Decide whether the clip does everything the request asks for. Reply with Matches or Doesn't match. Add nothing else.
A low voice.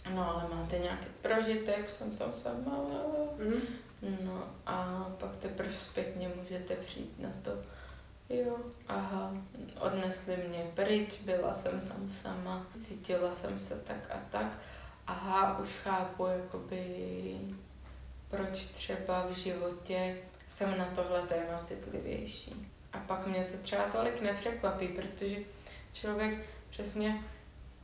Doesn't match